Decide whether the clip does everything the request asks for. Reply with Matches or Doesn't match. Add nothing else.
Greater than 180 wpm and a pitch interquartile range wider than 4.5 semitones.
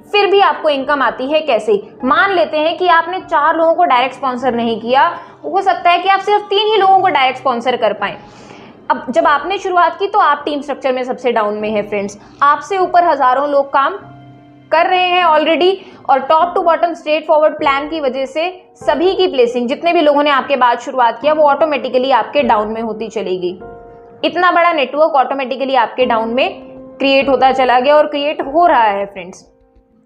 Matches